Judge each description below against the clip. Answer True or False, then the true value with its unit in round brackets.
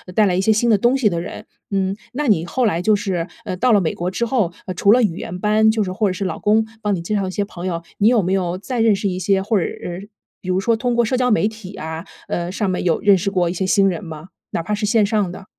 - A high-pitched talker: True (195 Hz)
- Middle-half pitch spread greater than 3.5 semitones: False (3.2 semitones)